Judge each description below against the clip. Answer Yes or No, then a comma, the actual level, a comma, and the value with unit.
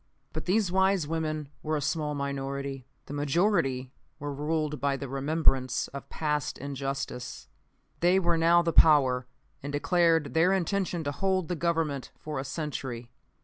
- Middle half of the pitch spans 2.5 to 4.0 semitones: Yes, average, 3.6 semitones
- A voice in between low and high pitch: Yes, medium, 150 Hz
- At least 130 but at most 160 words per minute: Yes, average, 150 wpm